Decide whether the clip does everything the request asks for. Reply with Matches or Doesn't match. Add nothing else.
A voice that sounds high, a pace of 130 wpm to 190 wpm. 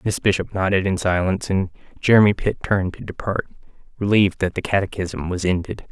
Doesn't match